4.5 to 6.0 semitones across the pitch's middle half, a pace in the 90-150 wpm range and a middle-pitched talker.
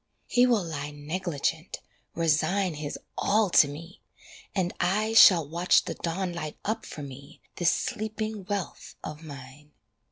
Yes: average, 5.1 semitones; average, 140 wpm; medium, 170 Hz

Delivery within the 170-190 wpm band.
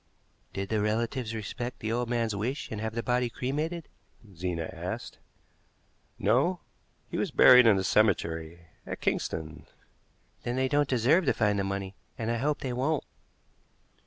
No: average, 160 wpm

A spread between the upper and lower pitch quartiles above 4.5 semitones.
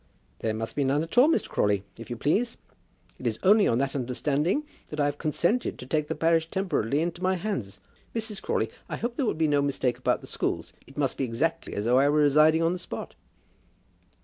Yes: average, 5.2 semitones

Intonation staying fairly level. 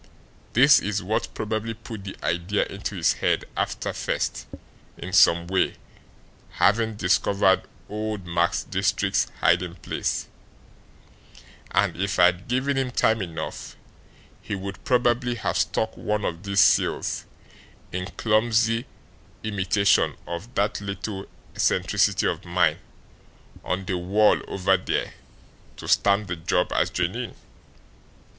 No: average, 3.4 semitones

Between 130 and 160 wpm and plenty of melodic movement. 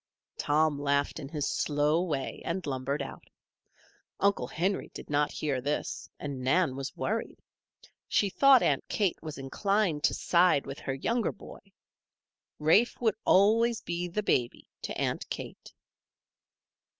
Yes: average, 140 wpm; wide, 5.7 semitones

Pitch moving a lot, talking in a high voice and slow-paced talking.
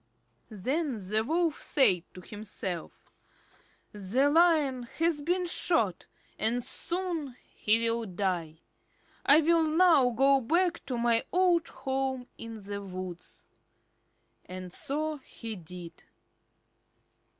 Yes: wide, 7.6 semitones; very high, 250 Hz; slow, 110 wpm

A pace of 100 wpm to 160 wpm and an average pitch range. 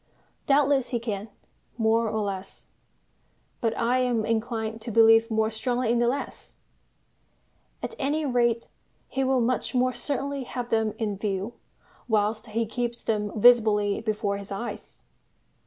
No: average, 140 wpm; narrow, 2.2 semitones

